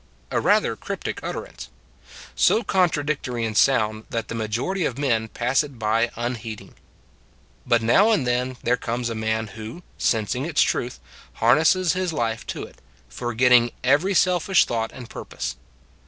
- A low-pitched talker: Yes, low, 120 Hz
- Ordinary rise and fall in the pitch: Yes, average, 4.7 semitones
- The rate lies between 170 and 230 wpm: No, average, 155 wpm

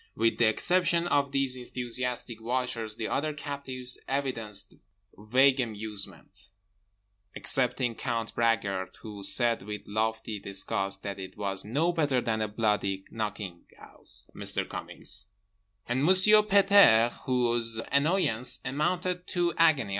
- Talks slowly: Yes, slow, 125 wpm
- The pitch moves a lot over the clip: No, average, 5.0 semitones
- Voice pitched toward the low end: Yes, low, 115 Hz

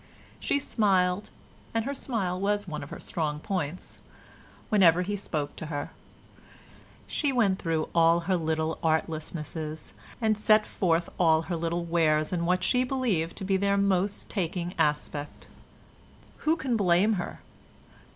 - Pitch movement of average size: Yes, average, 4.1 semitones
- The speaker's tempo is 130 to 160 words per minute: Yes, average, 145 wpm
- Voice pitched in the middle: Yes, medium, 180 Hz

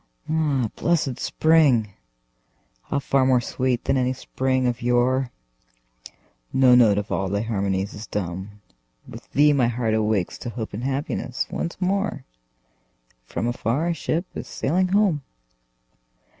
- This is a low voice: Yes, low, 125 Hz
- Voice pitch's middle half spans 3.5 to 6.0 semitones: Yes, average, 5.0 semitones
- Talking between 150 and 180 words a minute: No, average, 140 wpm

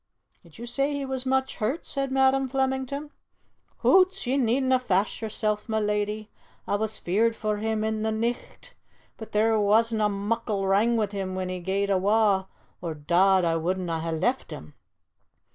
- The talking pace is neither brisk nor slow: Yes, average, 165 wpm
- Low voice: No, high, 215 Hz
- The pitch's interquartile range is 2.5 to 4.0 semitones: No, average, 4.5 semitones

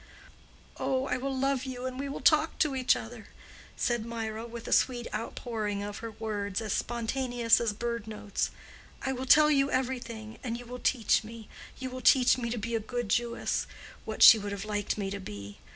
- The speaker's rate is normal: Yes, average, 195 wpm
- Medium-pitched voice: No, high, 235 Hz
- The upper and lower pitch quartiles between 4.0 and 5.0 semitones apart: No, average, 3.0 semitones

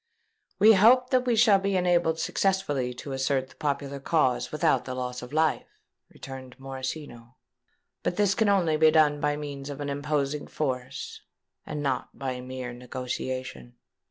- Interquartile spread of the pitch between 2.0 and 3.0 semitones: No, average, 3.9 semitones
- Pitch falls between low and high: Yes, medium, 145 Hz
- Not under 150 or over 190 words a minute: Yes, average, 155 wpm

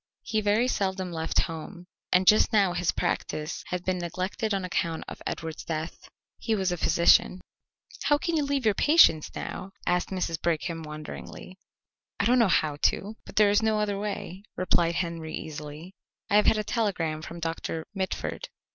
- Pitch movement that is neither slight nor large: Yes, average, 4.2 semitones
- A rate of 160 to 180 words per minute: Yes, average, 175 wpm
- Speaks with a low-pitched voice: No, medium, 185 Hz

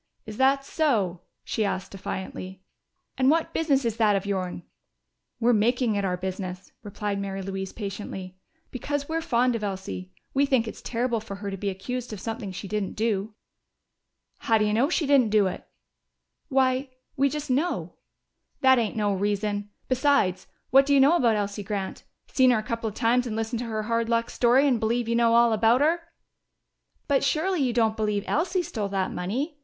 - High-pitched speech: Yes, high, 225 Hz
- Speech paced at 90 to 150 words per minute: No, average, 190 wpm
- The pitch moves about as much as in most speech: Yes, average, 4.4 semitones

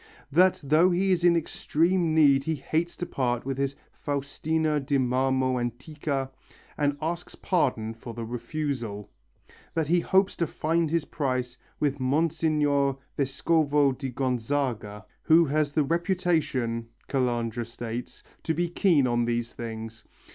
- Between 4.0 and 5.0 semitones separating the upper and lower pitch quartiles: Yes, average, 4.5 semitones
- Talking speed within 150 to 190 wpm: No, average, 140 wpm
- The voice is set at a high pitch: No, medium, 140 Hz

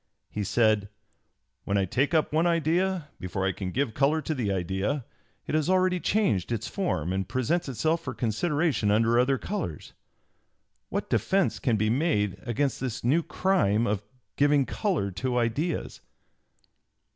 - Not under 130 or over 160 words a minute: Yes, average, 155 wpm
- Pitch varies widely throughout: Yes, wide, 7.5 semitones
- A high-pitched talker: No, low, 130 Hz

